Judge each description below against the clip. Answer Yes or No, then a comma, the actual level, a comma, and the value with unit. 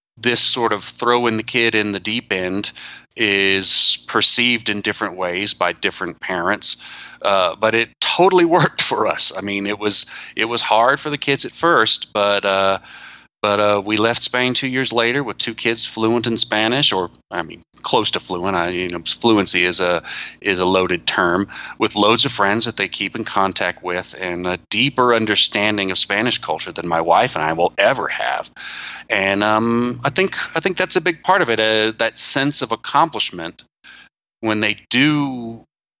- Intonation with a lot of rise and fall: No, average, 3.7 semitones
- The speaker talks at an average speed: Yes, average, 190 wpm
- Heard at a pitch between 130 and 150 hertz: No, low, 110 Hz